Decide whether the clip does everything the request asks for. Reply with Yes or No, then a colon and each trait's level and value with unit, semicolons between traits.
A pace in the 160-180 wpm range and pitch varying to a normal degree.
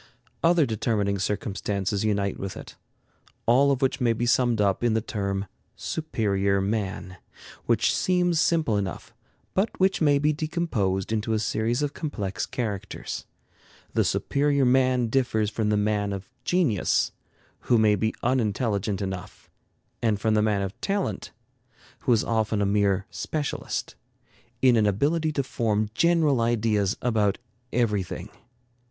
No: average, 140 wpm; average, 4.7 semitones